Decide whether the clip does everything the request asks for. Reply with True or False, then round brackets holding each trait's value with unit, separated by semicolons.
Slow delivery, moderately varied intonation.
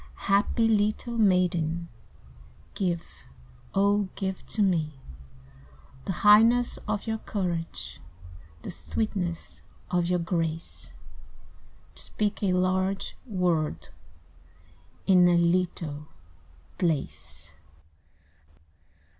True (85 wpm; 3.6 semitones)